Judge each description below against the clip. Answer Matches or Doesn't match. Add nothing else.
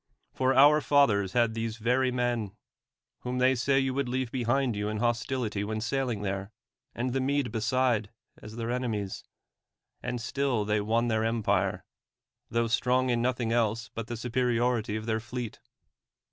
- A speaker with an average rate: Matches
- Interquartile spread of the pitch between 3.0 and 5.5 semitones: Doesn't match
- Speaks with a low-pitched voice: Matches